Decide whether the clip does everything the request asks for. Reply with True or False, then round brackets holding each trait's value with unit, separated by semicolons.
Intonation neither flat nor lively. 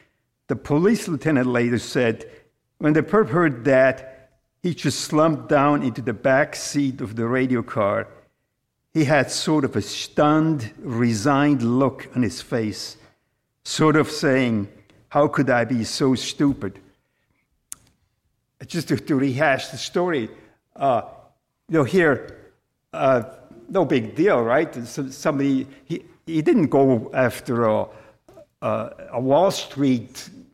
True (3.8 semitones)